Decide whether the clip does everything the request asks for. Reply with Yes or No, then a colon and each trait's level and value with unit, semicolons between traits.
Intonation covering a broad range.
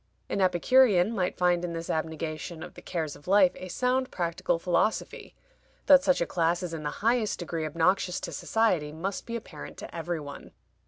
No: average, 3.8 semitones